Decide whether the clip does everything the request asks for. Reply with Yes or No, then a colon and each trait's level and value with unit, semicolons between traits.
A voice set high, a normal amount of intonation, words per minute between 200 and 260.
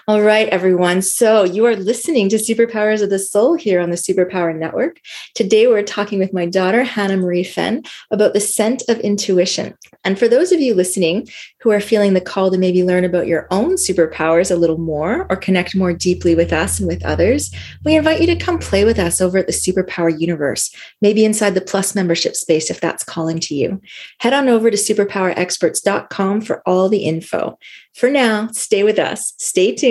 Yes: high, 195 Hz; average, 3.4 semitones; fast, 205 wpm